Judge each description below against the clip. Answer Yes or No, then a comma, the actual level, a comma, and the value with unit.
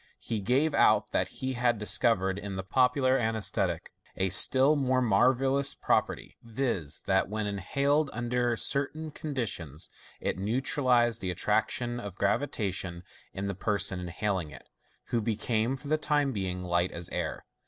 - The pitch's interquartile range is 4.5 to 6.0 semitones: Yes, wide, 5.4 semitones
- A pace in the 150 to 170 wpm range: Yes, average, 155 wpm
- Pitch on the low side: Yes, low, 115 Hz